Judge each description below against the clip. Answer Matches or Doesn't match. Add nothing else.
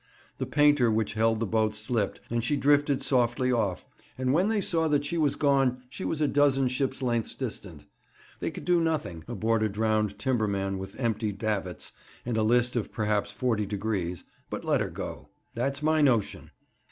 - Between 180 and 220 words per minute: Matches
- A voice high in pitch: Doesn't match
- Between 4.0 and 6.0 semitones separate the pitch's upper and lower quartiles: Matches